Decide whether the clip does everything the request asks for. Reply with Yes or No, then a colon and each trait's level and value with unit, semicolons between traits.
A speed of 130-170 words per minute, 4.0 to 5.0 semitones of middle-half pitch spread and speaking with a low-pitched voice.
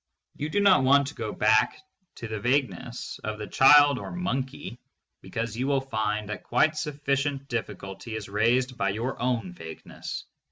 Yes: average, 165 wpm; average, 4.6 semitones; low, 125 Hz